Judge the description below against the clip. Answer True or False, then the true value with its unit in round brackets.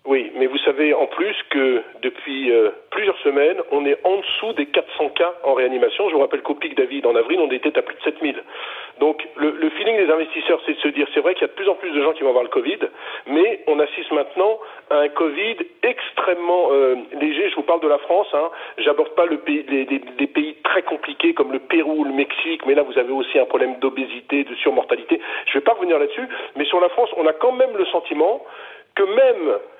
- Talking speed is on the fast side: True (245 wpm)